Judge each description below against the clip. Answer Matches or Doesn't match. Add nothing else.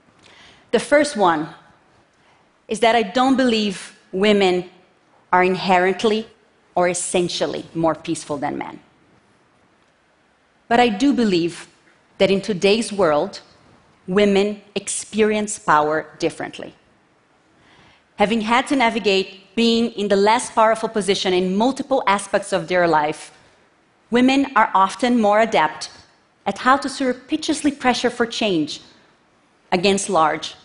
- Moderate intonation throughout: Matches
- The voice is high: Matches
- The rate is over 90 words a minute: Matches